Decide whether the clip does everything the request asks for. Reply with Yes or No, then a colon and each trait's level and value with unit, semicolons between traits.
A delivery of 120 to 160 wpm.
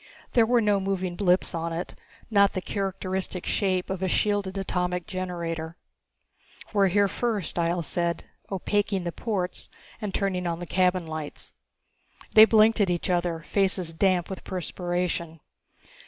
Yes: average, 145 wpm